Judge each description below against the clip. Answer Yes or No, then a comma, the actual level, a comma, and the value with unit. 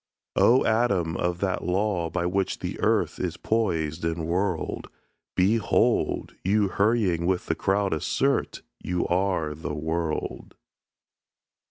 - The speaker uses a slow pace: Yes, slow, 125 wpm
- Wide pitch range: No, average, 3.2 semitones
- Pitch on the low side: Yes, very low, 90 Hz